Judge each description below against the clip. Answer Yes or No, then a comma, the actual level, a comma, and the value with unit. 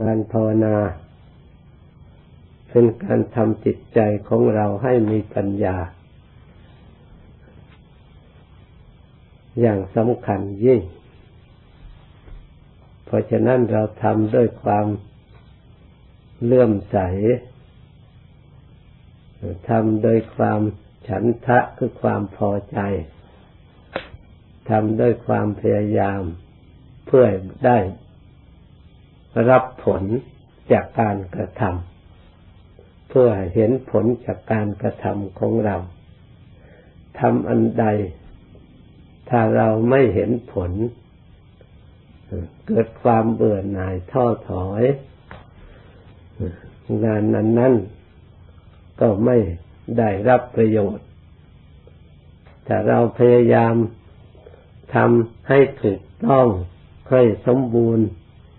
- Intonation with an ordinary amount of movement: Yes, average, 3.9 semitones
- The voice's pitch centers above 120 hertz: No, low, 105 Hz